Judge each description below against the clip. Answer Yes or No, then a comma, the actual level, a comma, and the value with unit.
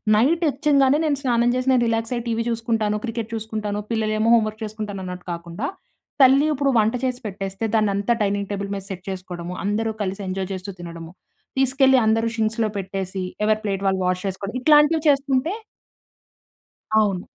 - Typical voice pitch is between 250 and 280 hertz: No, high, 215 Hz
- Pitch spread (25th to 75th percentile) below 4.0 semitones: No, average, 4.3 semitones